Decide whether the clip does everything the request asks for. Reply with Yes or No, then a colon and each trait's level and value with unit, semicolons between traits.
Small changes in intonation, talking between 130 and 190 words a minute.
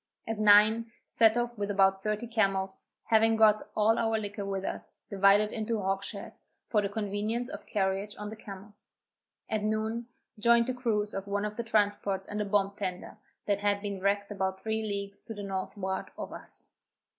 Yes: narrow, 1.8 semitones; average, 180 wpm